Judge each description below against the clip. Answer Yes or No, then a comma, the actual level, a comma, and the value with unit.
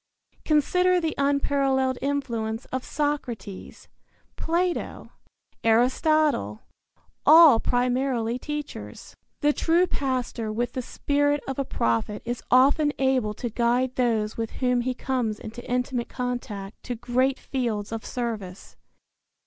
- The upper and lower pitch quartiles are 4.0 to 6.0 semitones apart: No, average, 3.5 semitones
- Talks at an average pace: No, slow, 115 wpm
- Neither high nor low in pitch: No, very high, 250 Hz